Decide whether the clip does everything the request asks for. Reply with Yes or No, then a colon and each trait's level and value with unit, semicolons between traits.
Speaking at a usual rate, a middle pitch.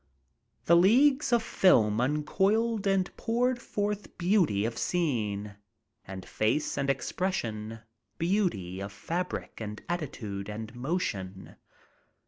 No: slow, 110 wpm; medium, 150 Hz